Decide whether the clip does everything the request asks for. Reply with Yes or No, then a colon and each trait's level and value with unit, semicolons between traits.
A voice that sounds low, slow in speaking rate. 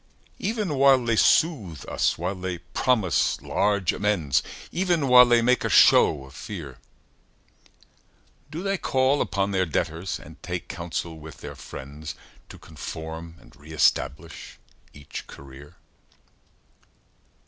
Yes: very low, 90 Hz; slow, 125 wpm